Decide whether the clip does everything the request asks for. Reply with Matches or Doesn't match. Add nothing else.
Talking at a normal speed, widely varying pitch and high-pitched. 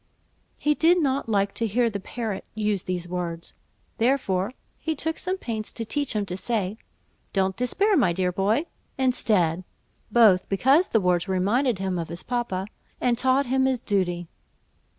Matches